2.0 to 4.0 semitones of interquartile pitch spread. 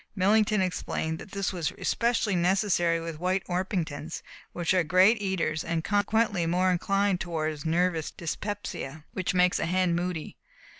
Yes: average, 2.8 semitones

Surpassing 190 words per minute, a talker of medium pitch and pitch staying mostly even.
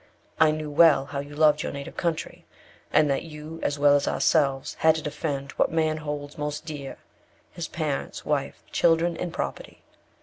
No: average, 175 wpm; medium, 150 Hz; narrow, 1.8 semitones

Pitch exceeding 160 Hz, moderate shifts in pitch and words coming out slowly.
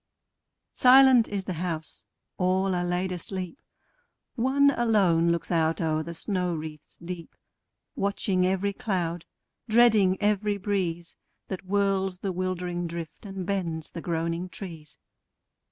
Yes: medium, 185 Hz; average, 3.0 semitones; slow, 125 wpm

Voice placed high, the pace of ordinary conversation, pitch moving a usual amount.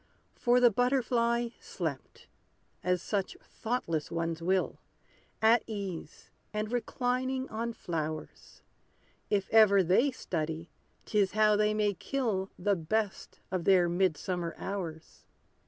No: high, 200 Hz; slow, 120 wpm; average, 5.0 semitones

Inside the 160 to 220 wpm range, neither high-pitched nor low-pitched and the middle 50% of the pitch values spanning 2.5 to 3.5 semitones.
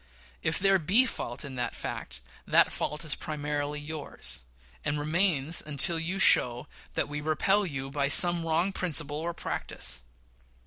Yes: average, 165 wpm; medium, 155 Hz; average, 3.0 semitones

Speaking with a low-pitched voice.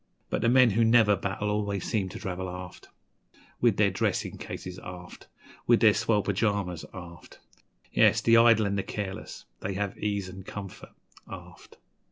Yes: low, 100 Hz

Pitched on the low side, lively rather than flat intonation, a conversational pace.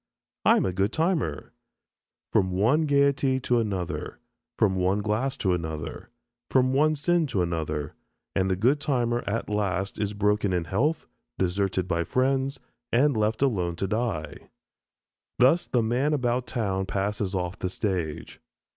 Yes: low, 105 Hz; wide, 5.8 semitones; average, 150 wpm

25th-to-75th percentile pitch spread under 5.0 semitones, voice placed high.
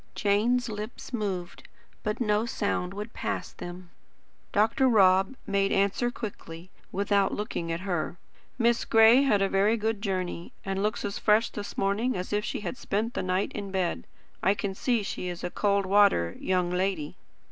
Yes: average, 2.7 semitones; high, 200 Hz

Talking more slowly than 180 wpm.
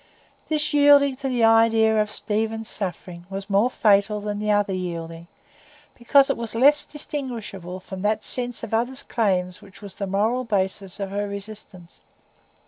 Yes: average, 160 wpm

